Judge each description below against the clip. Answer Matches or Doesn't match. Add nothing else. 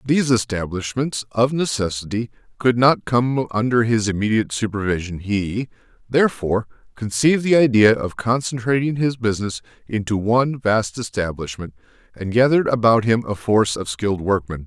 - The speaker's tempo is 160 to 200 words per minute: Doesn't match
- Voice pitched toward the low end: Matches